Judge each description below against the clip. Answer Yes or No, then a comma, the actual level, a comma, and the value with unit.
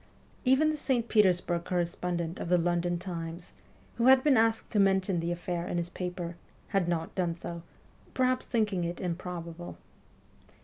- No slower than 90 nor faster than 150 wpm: No, average, 160 wpm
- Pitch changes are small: No, average, 3.6 semitones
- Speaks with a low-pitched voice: No, medium, 180 Hz